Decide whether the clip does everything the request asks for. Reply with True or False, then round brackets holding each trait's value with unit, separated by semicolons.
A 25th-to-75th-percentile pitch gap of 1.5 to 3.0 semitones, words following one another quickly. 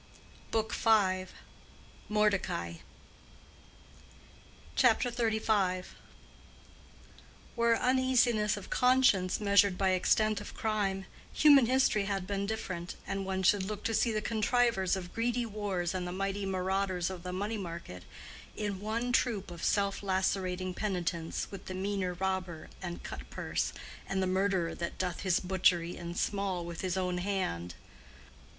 False (2.7 semitones; 135 wpm)